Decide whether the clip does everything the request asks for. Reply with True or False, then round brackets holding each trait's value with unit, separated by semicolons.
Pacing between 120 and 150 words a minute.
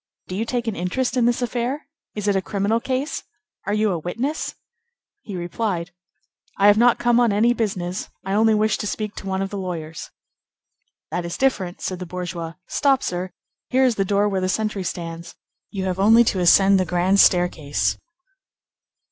False (190 wpm)